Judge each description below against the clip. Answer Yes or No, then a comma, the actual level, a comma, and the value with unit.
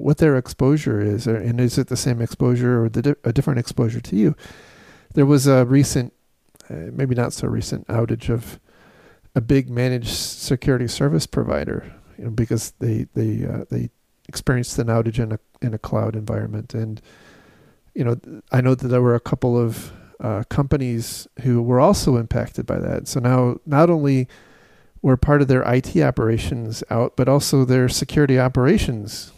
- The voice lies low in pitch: Yes, low, 125 Hz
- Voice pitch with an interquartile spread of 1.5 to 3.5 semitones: Yes, average, 2.9 semitones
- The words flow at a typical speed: Yes, average, 180 wpm